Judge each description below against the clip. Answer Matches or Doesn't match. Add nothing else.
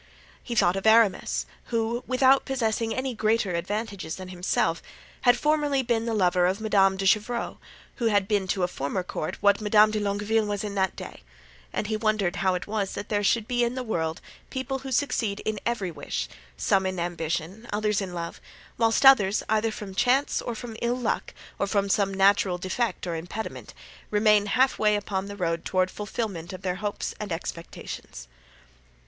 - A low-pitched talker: Doesn't match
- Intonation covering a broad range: Doesn't match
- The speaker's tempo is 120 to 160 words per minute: Doesn't match